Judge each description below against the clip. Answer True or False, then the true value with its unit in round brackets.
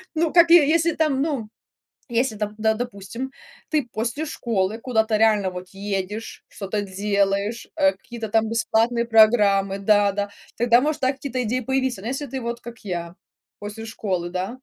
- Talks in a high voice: True (225 Hz)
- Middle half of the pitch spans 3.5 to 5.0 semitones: True (4.1 semitones)